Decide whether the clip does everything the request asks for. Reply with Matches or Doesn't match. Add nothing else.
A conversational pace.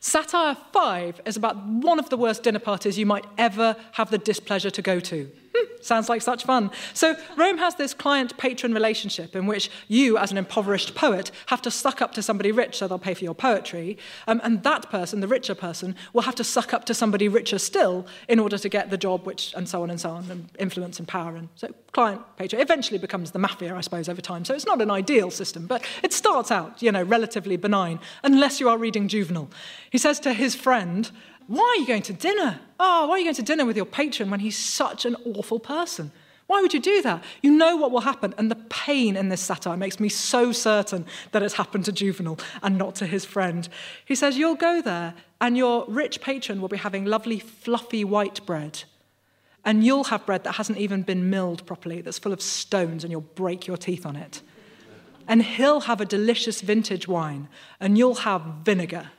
Doesn't match